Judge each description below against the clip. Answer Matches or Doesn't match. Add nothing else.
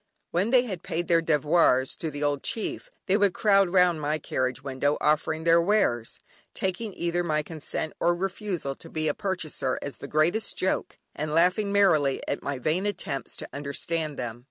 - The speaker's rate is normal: Matches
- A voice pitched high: Doesn't match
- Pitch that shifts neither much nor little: Matches